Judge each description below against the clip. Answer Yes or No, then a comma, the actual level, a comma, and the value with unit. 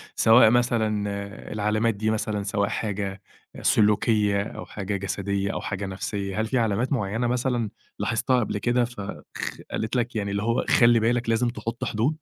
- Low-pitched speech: Yes, low, 110 Hz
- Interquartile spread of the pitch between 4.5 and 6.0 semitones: No, average, 2.7 semitones